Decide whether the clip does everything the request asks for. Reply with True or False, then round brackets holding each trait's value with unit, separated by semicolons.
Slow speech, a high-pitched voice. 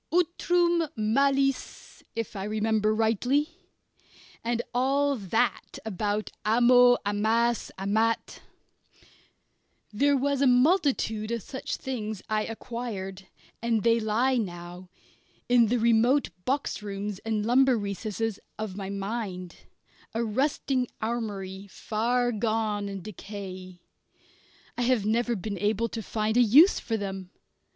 True (120 wpm; 225 Hz)